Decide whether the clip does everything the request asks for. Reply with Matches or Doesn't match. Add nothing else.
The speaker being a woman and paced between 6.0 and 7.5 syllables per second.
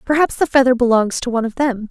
Matches